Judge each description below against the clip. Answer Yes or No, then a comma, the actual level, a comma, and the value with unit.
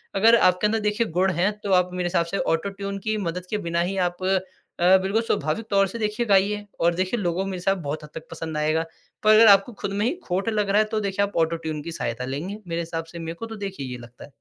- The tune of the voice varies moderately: Yes, average, 3.8 semitones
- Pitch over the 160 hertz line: Yes, high, 190 Hz